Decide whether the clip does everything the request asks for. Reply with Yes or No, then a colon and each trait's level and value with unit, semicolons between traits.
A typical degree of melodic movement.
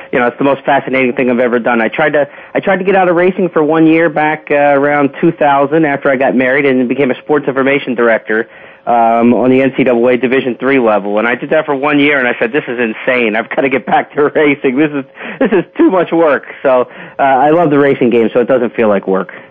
Yes: average, 3.4 semitones